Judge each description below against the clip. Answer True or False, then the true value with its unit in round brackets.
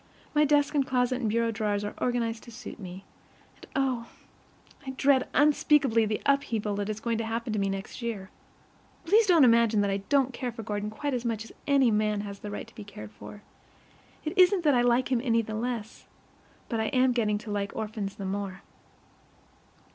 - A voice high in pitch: True (230 Hz)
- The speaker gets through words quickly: True (215 wpm)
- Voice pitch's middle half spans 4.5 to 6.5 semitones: False (3.7 semitones)